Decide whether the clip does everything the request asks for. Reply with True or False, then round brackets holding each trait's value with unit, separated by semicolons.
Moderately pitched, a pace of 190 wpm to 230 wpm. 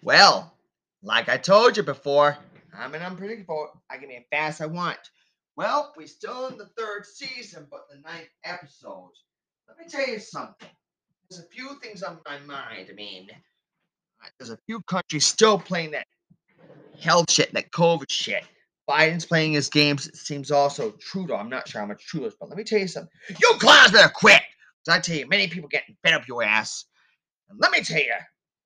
True (170 Hz; 205 wpm)